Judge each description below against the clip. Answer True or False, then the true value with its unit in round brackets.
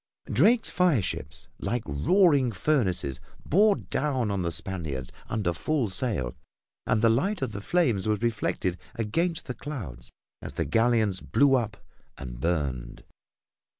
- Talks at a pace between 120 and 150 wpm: True (140 wpm)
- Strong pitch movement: True (8.5 semitones)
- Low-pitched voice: True (110 Hz)